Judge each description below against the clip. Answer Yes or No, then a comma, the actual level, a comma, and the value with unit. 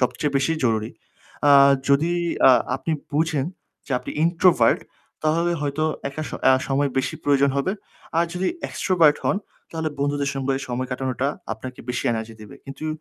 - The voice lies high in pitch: No, medium, 140 Hz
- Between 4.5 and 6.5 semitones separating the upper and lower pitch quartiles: No, average, 3.4 semitones